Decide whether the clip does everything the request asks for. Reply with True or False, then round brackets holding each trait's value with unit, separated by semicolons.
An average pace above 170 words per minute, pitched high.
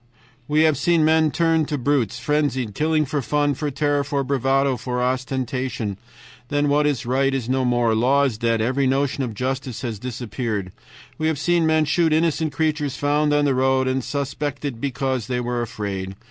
False (180 wpm; 135 Hz)